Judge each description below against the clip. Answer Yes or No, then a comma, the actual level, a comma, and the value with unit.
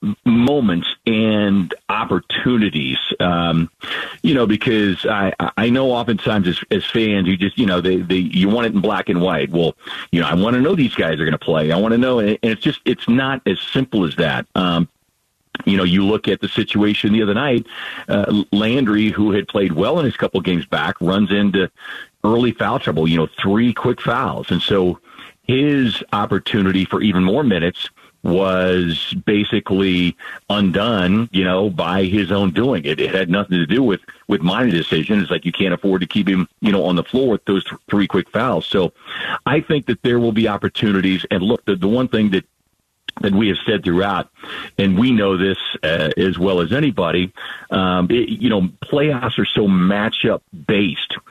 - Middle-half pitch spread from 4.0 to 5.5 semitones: No, average, 3.4 semitones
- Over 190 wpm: Yes, average, 200 wpm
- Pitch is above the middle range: No, low, 100 Hz